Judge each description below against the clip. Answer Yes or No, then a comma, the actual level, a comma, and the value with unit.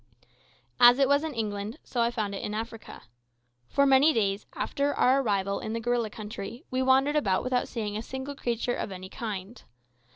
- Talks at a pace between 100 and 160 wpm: No, average, 190 wpm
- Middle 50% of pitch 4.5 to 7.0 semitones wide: No, average, 4.1 semitones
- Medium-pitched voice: No, high, 235 Hz